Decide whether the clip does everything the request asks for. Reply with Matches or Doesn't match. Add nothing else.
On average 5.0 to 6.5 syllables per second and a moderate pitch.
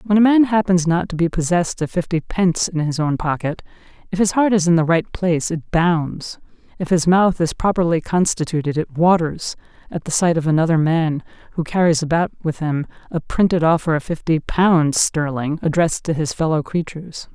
Matches